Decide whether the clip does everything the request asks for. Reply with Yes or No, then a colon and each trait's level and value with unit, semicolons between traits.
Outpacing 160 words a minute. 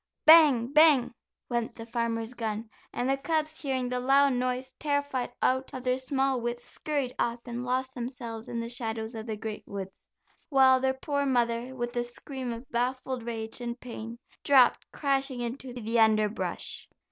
Yes: average, 170 wpm